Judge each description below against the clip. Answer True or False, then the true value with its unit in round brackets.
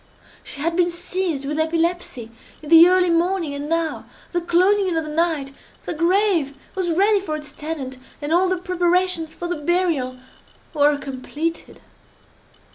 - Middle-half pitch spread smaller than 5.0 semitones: True (3.2 semitones)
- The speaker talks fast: False (165 wpm)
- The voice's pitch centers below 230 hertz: False (335 Hz)